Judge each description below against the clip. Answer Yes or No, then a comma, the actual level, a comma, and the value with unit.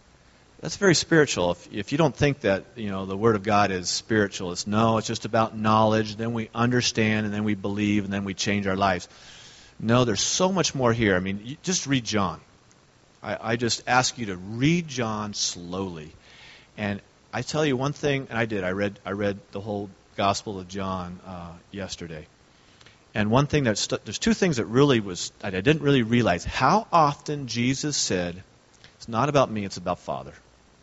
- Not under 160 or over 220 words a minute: Yes, average, 200 wpm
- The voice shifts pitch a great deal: No, average, 4.6 semitones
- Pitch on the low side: Yes, low, 110 Hz